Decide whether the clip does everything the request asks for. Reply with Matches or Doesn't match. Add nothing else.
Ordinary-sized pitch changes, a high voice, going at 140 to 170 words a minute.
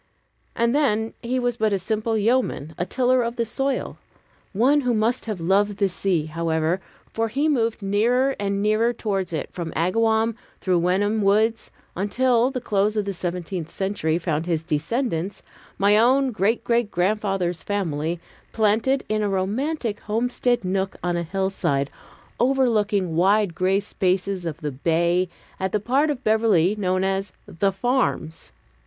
Matches